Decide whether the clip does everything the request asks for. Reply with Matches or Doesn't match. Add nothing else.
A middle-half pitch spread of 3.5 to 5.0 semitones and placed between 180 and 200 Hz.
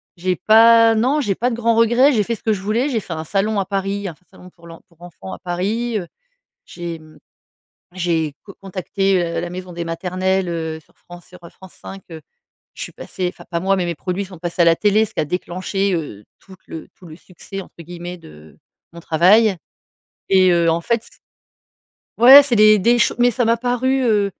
Matches